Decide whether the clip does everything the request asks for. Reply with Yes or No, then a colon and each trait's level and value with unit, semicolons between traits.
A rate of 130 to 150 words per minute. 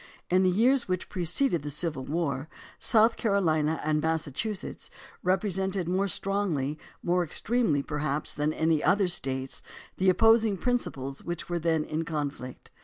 Yes: average, 140 wpm